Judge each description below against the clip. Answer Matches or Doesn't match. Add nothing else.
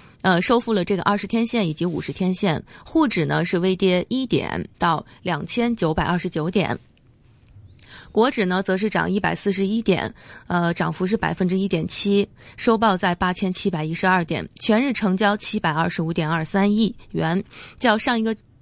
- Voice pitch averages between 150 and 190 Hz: Matches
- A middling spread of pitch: Matches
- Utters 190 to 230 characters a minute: Doesn't match